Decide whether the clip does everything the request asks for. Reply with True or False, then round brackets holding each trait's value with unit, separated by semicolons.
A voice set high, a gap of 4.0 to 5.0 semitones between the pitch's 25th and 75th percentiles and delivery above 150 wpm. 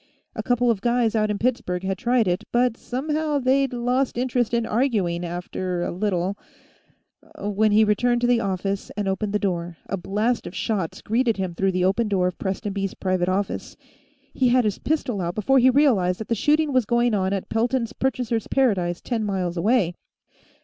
True (215 Hz; 4.5 semitones; 190 wpm)